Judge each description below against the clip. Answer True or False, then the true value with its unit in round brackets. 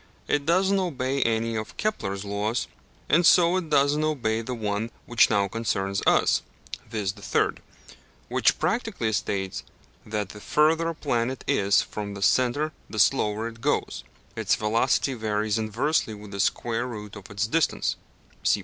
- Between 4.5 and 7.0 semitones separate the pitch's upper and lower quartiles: True (5.6 semitones)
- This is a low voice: True (115 Hz)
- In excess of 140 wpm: True (165 wpm)